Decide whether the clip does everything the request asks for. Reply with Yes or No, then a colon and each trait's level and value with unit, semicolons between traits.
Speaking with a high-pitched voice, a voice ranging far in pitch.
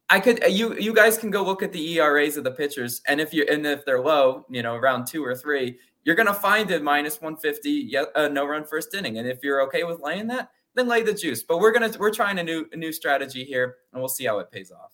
No: medium, 155 Hz; wide, 7.1 semitones